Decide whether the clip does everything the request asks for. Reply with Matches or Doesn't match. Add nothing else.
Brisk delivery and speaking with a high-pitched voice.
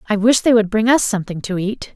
Matches